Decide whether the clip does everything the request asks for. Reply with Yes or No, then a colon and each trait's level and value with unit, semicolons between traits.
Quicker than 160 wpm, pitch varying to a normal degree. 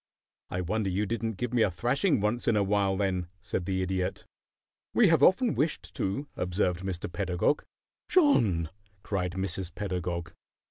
No: average, 155 wpm; average, 4.1 semitones